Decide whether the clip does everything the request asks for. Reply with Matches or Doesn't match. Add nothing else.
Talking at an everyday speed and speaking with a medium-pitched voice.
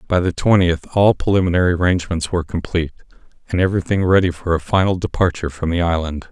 Doesn't match